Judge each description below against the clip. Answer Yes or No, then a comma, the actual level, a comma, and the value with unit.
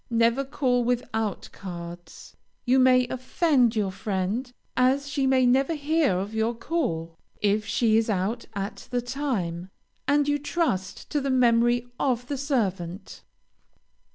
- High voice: Yes, high, 240 Hz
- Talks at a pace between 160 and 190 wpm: No, average, 140 wpm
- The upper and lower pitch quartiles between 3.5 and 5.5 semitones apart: Yes, average, 5.0 semitones